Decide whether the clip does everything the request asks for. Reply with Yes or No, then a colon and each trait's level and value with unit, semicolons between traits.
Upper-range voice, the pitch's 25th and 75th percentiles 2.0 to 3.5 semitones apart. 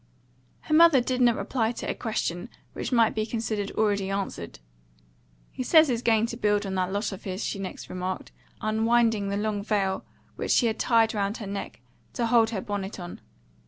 Yes: high, 215 Hz; average, 2.8 semitones